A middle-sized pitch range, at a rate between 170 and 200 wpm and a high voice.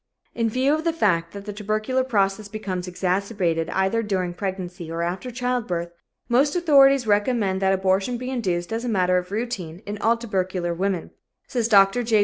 Yes: average, 4.5 semitones; average, 175 wpm; high, 200 Hz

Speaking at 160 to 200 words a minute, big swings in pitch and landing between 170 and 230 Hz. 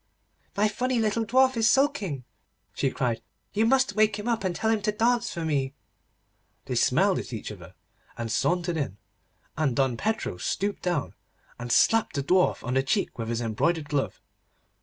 Yes: average, 180 wpm; wide, 8.6 semitones; medium, 185 Hz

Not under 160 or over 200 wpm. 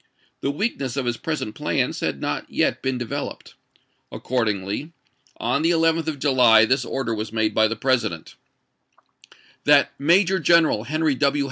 No: average, 150 wpm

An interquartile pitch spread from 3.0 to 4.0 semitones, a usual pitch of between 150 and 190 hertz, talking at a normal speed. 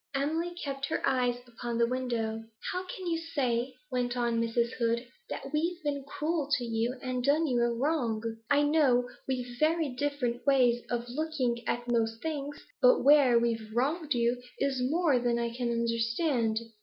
No: average, 3.6 semitones; very high, 250 Hz; average, 170 wpm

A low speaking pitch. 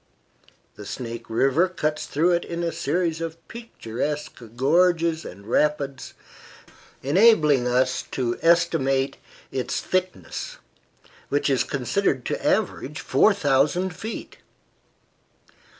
No: medium, 150 Hz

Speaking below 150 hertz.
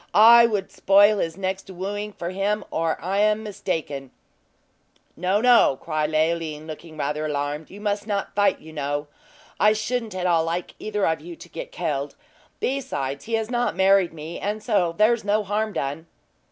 No: high, 190 Hz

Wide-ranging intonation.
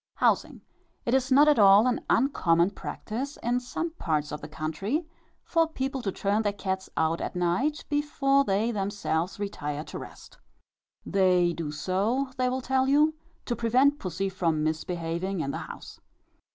Yes: wide, 7.3 semitones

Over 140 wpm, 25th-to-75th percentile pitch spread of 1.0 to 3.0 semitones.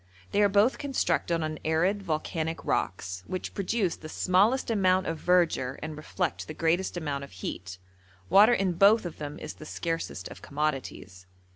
No: average, 165 wpm; average, 4.0 semitones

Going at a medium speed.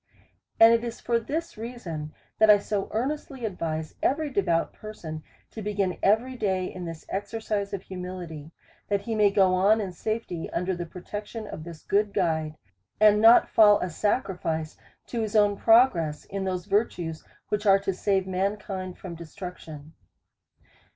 Yes: average, 165 wpm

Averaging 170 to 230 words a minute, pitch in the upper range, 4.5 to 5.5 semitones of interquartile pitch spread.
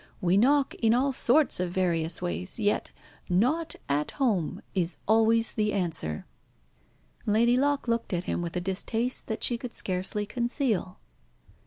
No: average, 150 wpm; high, 210 Hz; average, 5.0 semitones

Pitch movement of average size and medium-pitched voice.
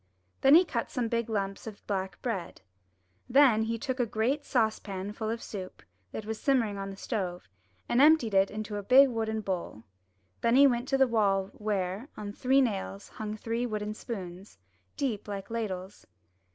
No: average, 3.5 semitones; high, 220 Hz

